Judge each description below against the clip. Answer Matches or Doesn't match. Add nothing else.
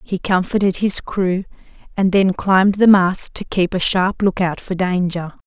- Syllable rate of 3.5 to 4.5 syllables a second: Matches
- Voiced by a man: Doesn't match